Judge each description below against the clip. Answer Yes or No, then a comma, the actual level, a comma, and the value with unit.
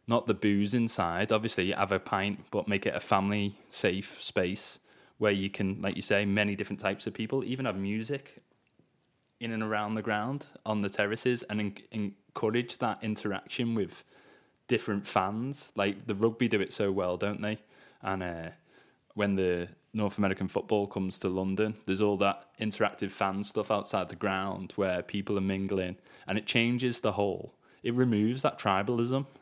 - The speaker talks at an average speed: Yes, average, 175 wpm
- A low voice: Yes, low, 105 Hz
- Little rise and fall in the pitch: Yes, narrow, 2.3 semitones